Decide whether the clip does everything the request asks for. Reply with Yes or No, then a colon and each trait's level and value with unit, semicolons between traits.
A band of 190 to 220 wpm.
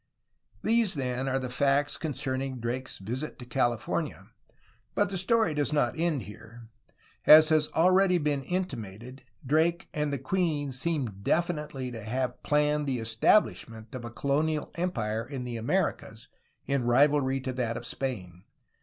No: average, 150 wpm